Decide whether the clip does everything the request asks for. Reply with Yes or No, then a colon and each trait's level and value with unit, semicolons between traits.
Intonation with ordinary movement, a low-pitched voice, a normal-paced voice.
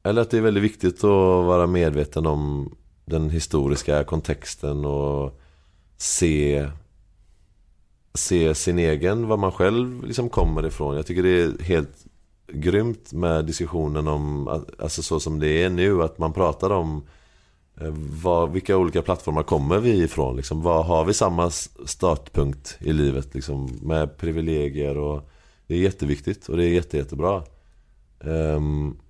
Yes: average, 3.5 semitones; very low, 80 Hz; average, 145 wpm